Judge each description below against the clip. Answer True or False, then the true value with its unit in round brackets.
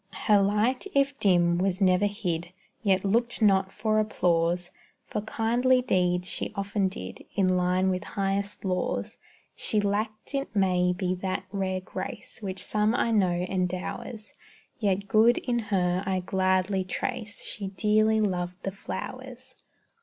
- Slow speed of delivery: False (145 wpm)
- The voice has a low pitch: False (195 Hz)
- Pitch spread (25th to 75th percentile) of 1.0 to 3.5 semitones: True (2.7 semitones)